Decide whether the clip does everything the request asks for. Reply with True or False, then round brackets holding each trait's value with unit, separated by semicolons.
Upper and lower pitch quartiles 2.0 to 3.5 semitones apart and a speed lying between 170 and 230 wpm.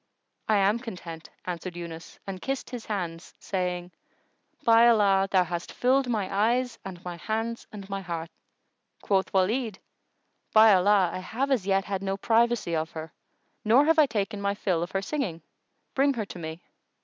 False (4.2 semitones; 175 wpm)